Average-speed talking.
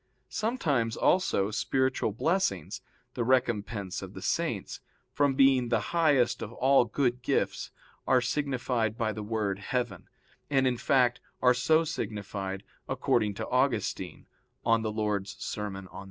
No: slow, 130 wpm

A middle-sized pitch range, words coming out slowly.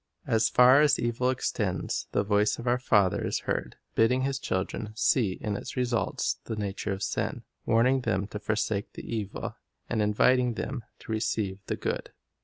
No: average, 3.3 semitones; average, 175 wpm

